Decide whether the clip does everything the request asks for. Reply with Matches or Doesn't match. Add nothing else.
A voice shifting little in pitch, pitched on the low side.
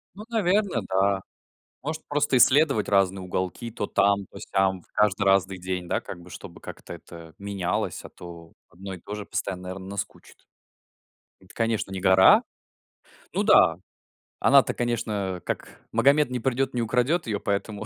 Doesn't match